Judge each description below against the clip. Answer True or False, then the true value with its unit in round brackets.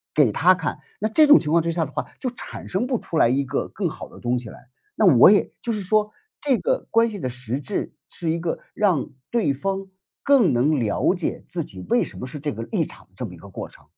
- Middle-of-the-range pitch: True (170 Hz)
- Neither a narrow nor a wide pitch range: False (7.6 semitones)